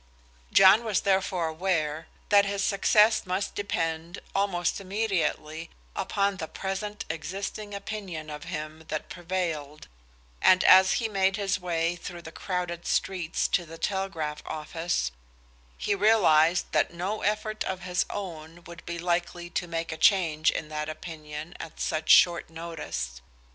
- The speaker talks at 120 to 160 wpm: Yes, average, 145 wpm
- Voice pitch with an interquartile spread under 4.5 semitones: Yes, average, 3.4 semitones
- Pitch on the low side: No, medium, 175 Hz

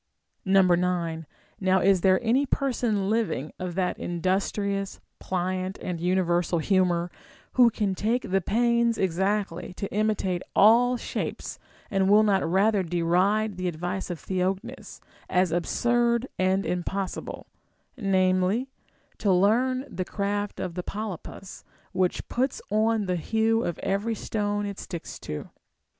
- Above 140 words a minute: No, slow, 135 wpm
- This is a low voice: No, high, 195 Hz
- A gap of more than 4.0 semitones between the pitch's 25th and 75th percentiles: No, average, 3.1 semitones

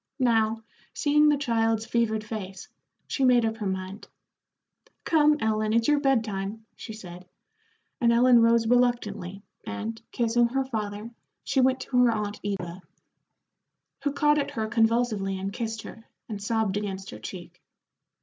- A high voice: Yes, high, 225 Hz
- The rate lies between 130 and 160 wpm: Yes, average, 150 wpm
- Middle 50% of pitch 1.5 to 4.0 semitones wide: Yes, average, 3.0 semitones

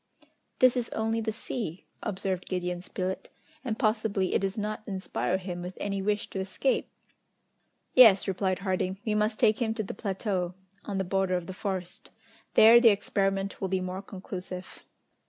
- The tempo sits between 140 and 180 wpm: Yes, average, 170 wpm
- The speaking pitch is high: Yes, high, 195 Hz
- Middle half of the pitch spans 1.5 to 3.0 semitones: Yes, narrow, 2.5 semitones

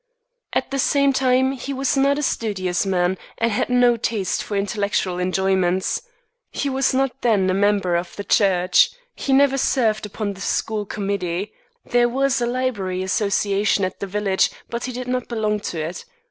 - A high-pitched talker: Yes, high, 210 Hz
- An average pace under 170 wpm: No, average, 180 wpm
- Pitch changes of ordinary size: Yes, average, 4.9 semitones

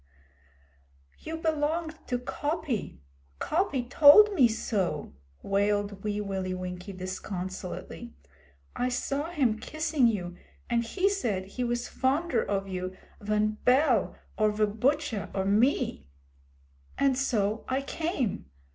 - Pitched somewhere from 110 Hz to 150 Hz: No, high, 230 Hz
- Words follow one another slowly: Yes, slow, 120 wpm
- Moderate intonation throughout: No, wide, 6.6 semitones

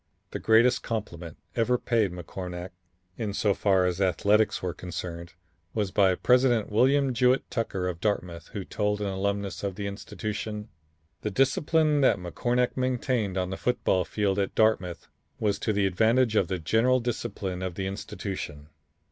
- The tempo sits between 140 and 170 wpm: Yes, average, 155 wpm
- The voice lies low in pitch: Yes, low, 100 Hz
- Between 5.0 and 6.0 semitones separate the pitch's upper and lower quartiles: No, average, 3.9 semitones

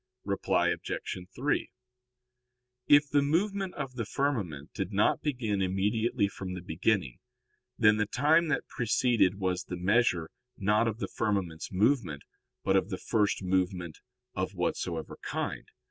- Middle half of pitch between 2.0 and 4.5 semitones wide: No, average, 5.2 semitones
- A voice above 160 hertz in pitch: No, low, 105 Hz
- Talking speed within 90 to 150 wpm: Yes, average, 140 wpm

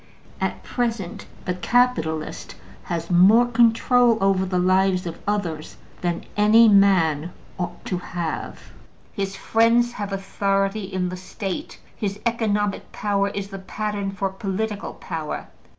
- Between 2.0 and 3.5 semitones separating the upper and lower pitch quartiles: Yes, average, 2.8 semitones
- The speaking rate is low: Yes, slow, 130 wpm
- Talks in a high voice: Yes, high, 195 Hz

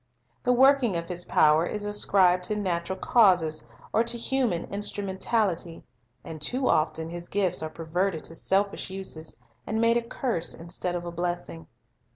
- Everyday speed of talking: Yes, average, 160 wpm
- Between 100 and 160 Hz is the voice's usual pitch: No, medium, 185 Hz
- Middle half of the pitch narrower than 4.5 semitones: Yes, average, 3.9 semitones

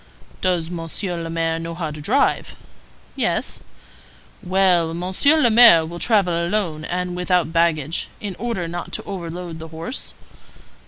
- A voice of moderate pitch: Yes, medium, 175 Hz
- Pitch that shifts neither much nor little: No, narrow, 2.1 semitones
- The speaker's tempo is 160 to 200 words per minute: No, average, 145 wpm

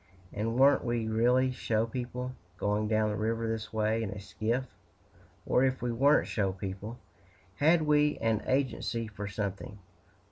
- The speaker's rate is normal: Yes, average, 155 wpm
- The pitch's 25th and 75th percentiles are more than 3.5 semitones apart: No, average, 3.1 semitones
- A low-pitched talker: Yes, low, 115 Hz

